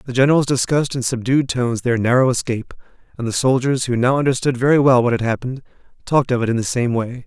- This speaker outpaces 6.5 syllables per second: Yes, 6.9 syllables/s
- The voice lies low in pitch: Yes, low, 125 Hz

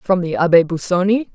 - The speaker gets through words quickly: No, average, 180 wpm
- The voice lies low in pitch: No, medium, 185 Hz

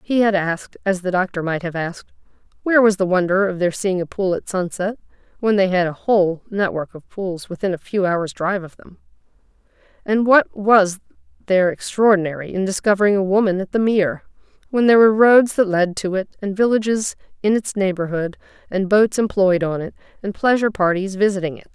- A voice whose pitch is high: Yes, high, 195 Hz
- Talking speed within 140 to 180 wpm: No, average, 195 wpm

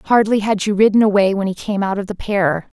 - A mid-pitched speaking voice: No, high, 200 Hz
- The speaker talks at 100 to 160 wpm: No, fast, 260 wpm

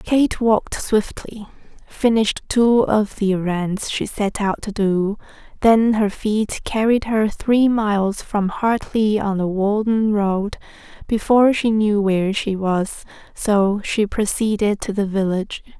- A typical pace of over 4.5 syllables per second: No, 3.9 syllables/s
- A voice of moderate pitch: No, high, 210 Hz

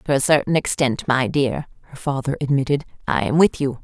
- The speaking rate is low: No, fast, 205 wpm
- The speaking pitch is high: No, low, 135 Hz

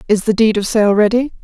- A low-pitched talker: No, high, 215 Hz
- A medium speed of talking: No, fast, 250 wpm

